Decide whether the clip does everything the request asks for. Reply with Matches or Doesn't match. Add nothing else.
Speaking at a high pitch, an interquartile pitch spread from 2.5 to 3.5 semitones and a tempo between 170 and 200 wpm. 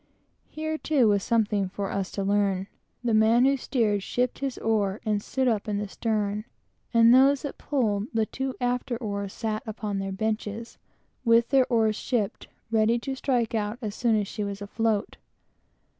Matches